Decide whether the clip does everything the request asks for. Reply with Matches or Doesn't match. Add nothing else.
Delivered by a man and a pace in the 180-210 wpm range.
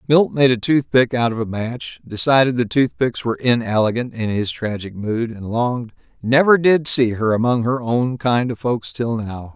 Matches